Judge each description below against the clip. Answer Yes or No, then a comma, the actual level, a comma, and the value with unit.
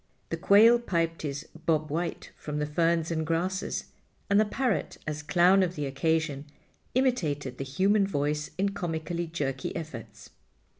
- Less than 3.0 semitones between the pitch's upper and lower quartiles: No, average, 4.1 semitones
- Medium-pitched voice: Yes, medium, 165 Hz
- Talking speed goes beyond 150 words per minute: No, average, 140 wpm